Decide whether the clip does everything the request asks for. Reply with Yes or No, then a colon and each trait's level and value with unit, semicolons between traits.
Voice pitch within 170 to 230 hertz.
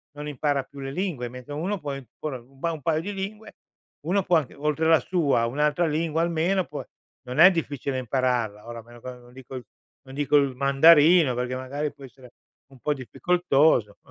No: medium, 145 Hz